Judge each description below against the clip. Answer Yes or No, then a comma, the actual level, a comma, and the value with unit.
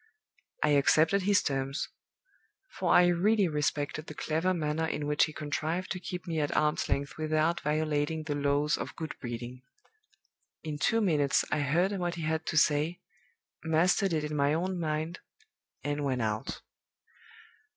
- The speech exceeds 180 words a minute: No, average, 160 wpm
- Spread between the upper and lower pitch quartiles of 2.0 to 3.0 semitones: Yes, average, 2.7 semitones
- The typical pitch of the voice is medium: Yes, medium, 155 Hz